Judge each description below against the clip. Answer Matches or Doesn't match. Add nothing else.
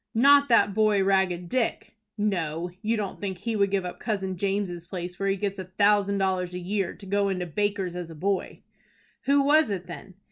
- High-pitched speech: Matches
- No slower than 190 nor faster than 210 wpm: Matches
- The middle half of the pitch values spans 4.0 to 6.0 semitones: Doesn't match